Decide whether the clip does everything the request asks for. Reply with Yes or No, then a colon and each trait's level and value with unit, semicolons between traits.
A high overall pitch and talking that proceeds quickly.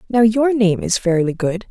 Yes: high, 210 Hz; fast, 210 wpm